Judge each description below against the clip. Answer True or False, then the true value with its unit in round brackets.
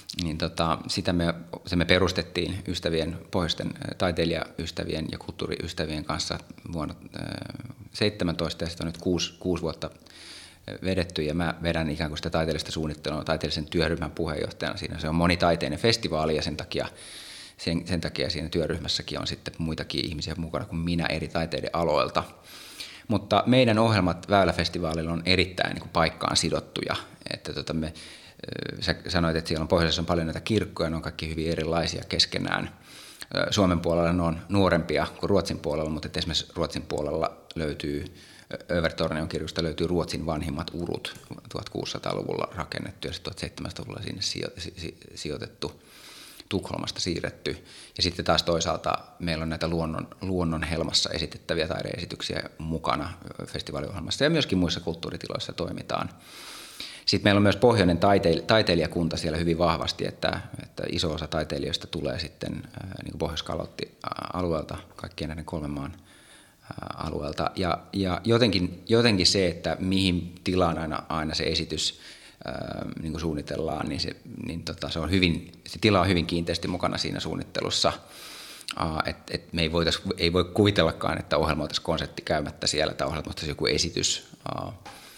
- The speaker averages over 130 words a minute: True (145 wpm)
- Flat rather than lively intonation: True (2.2 semitones)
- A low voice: True (85 Hz)